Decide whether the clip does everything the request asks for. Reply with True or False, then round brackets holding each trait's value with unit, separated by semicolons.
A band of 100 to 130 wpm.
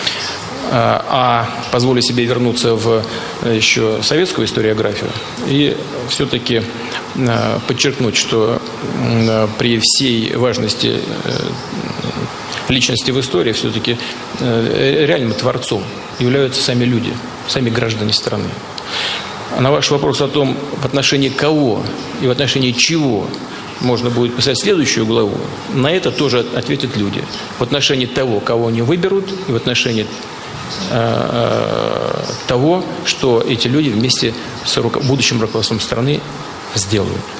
True (110 wpm)